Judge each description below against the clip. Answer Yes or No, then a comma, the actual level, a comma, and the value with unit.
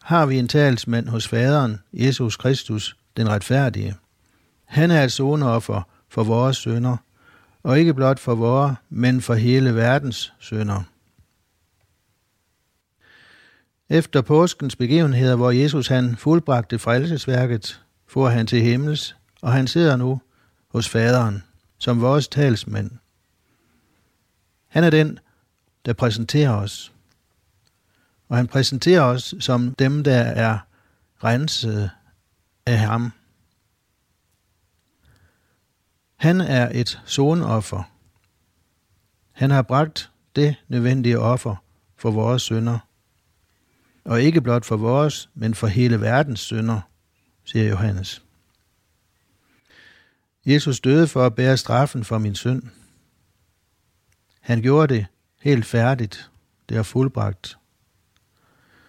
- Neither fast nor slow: No, slow, 110 wpm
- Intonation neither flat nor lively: Yes, average, 4.5 semitones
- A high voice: No, low, 115 Hz